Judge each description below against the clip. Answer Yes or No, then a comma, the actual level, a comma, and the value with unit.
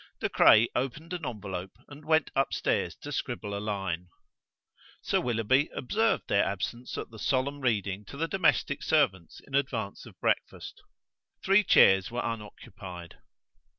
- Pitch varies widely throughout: Yes, wide, 6.2 semitones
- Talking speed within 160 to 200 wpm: No, average, 145 wpm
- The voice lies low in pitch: Yes, low, 120 Hz